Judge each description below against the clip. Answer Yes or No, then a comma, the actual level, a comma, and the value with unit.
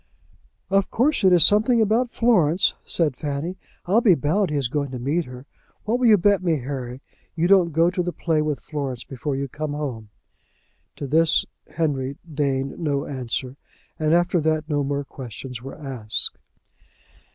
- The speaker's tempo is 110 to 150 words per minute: No, average, 175 wpm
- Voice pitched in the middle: Yes, medium, 150 Hz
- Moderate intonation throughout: Yes, average, 4.6 semitones